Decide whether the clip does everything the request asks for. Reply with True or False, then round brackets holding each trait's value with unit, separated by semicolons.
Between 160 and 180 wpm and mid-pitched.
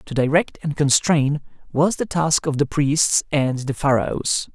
True (170 wpm; 145 Hz)